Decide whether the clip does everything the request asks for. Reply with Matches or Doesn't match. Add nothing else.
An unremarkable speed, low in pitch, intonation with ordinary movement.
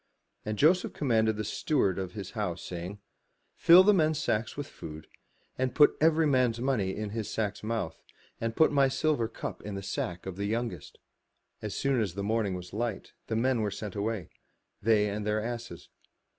Matches